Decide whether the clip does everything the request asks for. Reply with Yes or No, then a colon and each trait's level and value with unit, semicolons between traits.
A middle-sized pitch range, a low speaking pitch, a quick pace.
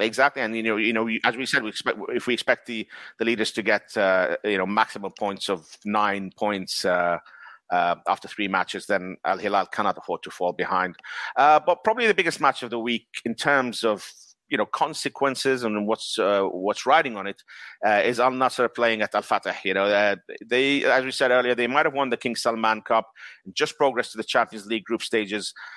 Yes: average, 3.8 semitones; low, 115 Hz; fast, 220 wpm